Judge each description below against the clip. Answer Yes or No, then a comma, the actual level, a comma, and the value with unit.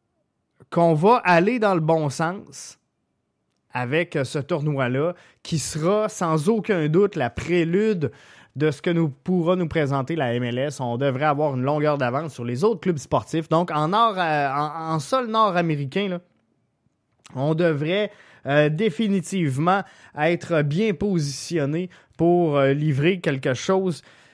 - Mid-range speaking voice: Yes, medium, 160 Hz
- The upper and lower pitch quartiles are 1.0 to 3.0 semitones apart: No, average, 4.3 semitones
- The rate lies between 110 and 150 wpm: Yes, slow, 145 wpm